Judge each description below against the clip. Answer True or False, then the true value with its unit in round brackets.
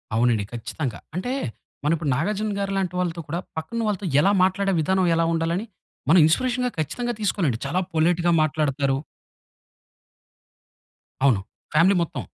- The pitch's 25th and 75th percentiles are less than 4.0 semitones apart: False (4.6 semitones)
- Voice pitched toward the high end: False (170 Hz)